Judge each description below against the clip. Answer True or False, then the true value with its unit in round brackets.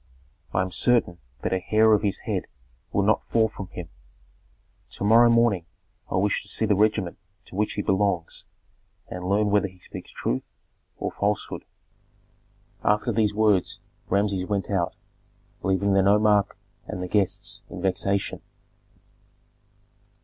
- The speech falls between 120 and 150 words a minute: True (145 wpm)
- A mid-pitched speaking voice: False (100 Hz)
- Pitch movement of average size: False (2.1 semitones)